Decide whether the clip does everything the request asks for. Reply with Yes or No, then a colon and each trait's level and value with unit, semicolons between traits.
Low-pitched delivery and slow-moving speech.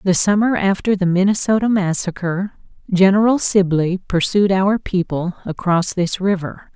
No: high, 190 Hz; slow, 125 wpm